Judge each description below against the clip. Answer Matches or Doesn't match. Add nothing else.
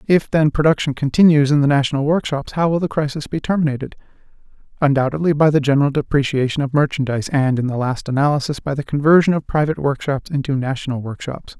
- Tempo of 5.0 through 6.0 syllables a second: Doesn't match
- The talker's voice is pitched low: Doesn't match